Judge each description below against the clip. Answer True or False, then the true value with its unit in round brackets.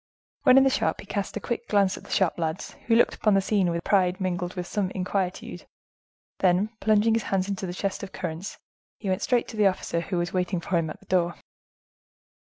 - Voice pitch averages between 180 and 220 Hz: True (190 Hz)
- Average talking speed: False (230 wpm)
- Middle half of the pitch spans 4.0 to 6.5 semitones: False (2.5 semitones)